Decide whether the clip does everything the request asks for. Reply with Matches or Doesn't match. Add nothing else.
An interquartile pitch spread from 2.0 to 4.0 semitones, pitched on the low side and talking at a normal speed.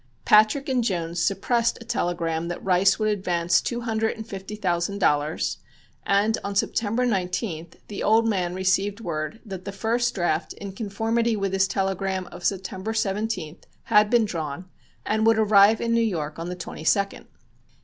Doesn't match